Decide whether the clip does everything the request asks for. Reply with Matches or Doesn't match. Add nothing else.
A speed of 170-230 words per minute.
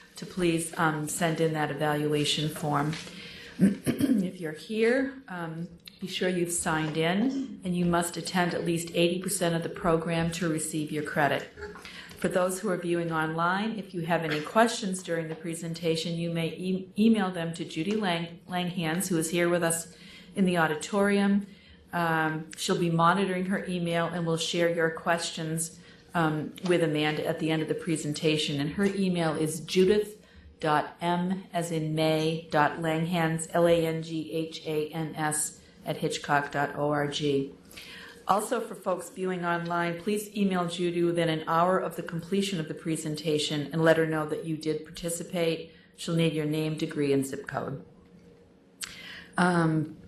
Doesn't match